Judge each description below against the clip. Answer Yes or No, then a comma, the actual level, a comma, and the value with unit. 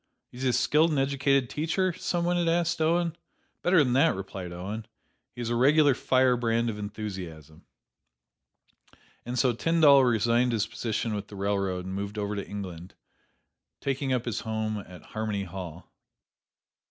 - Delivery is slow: No, average, 155 wpm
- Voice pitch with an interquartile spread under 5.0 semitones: No, wide, 5.6 semitones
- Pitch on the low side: Yes, low, 115 Hz